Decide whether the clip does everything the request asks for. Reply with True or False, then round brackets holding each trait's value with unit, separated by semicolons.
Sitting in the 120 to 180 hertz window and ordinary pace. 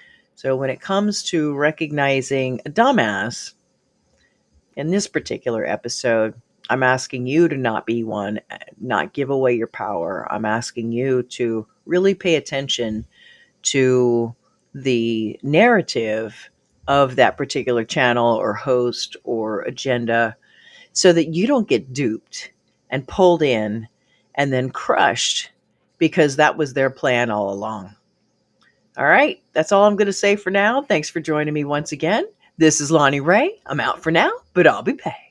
True (135 Hz; 150 wpm)